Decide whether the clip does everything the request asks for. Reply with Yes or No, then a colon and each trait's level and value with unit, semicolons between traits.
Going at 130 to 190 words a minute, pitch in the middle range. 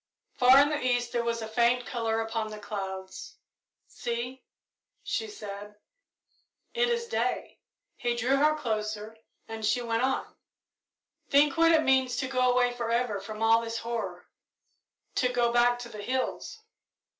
No: average, 155 wpm; high, 240 Hz